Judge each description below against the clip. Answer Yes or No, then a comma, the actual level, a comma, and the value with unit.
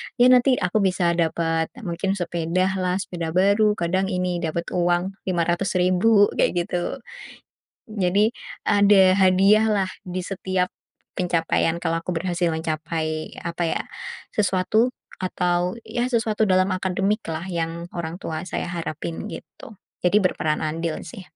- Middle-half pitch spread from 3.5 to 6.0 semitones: No, narrow, 2.6 semitones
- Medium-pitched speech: Yes, medium, 180 Hz